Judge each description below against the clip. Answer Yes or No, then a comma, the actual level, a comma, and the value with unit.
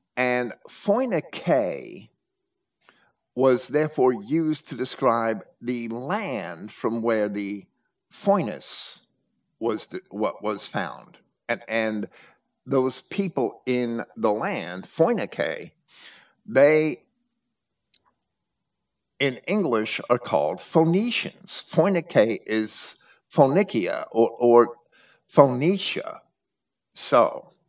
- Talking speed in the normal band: No, slow, 85 wpm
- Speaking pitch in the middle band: No, low, 130 Hz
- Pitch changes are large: Yes, wide, 7.6 semitones